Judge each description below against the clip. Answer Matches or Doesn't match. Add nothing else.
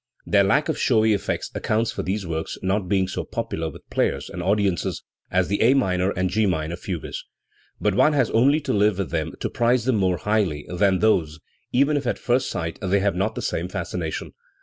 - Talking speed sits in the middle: Doesn't match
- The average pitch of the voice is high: Doesn't match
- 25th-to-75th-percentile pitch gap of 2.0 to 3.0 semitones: Doesn't match